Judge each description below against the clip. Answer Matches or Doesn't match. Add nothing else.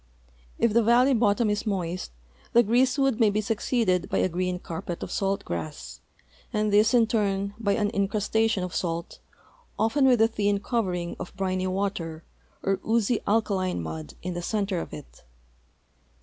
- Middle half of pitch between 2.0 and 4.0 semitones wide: Matches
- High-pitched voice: Matches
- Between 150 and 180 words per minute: Matches